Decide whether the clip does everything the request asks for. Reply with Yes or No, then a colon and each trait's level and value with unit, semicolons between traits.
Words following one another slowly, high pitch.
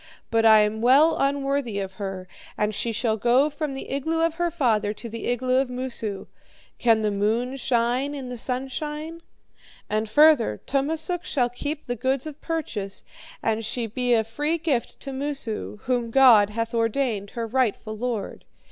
No: average, 170 wpm; high, 245 Hz